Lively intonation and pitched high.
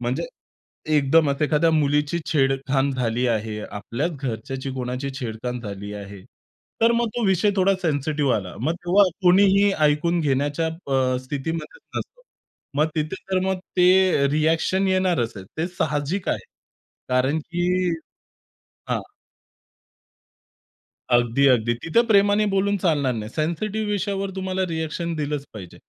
No: wide, 6.0 semitones; medium, 155 Hz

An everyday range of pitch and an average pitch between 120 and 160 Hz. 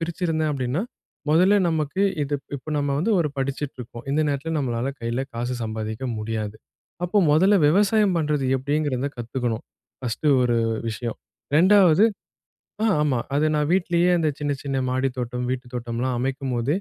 Yes: average, 4.3 semitones; medium, 140 Hz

